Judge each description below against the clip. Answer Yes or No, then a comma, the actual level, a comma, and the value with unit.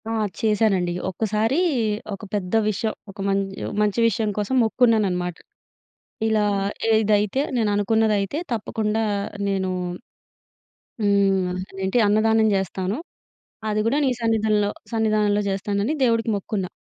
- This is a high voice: Yes, high, 210 Hz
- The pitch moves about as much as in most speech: No, narrow, 2.1 semitones